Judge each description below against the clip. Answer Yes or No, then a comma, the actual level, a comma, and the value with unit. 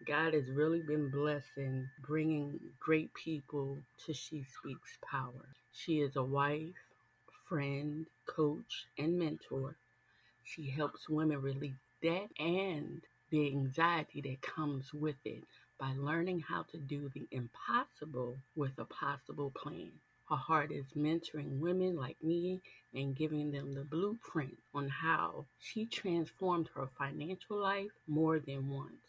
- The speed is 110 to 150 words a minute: Yes, slow, 135 wpm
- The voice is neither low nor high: Yes, medium, 150 Hz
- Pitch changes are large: No, average, 2.7 semitones